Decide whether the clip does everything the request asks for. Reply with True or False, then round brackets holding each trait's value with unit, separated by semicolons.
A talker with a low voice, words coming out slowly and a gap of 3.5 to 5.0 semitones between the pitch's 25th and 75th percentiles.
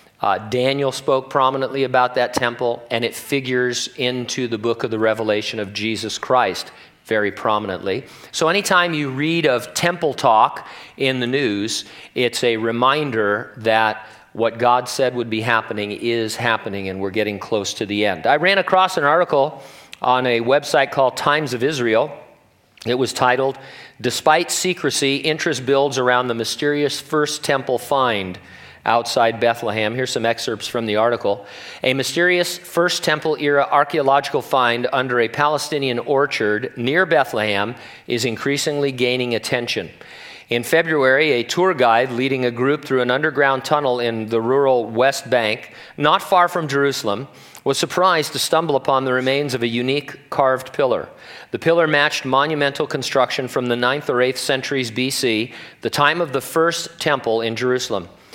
False (130 Hz; 155 wpm; 3.9 semitones)